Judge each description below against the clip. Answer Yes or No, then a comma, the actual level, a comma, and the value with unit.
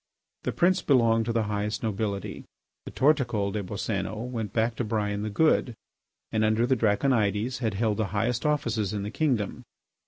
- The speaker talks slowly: No, average, 175 wpm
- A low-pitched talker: Yes, low, 110 Hz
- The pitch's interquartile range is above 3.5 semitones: No, average, 2.9 semitones